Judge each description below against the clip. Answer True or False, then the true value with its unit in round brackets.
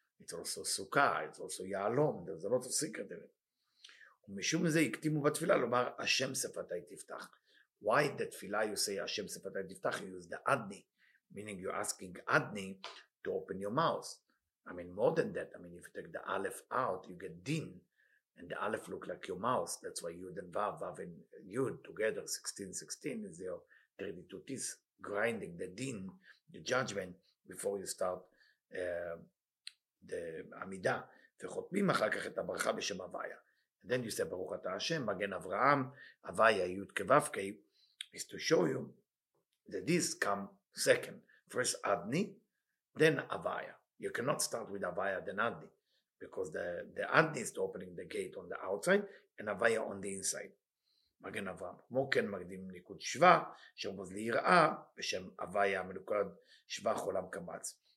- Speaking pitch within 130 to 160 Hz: False (200 Hz)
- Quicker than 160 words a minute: False (145 wpm)